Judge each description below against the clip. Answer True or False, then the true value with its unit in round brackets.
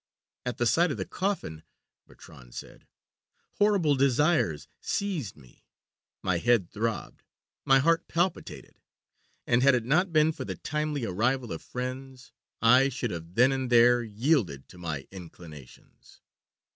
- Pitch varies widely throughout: True (8.0 semitones)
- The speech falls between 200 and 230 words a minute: False (140 wpm)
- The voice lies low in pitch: True (125 Hz)